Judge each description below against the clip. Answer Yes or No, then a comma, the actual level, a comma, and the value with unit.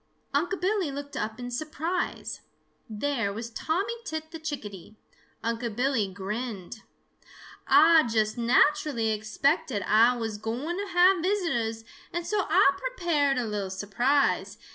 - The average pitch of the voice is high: Yes, very high, 250 Hz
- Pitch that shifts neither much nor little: No, wide, 6.5 semitones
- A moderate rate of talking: No, slow, 130 wpm